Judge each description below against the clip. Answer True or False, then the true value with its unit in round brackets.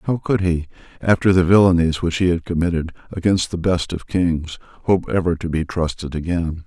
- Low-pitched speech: True (85 Hz)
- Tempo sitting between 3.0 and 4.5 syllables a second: False (5.4 syllables/s)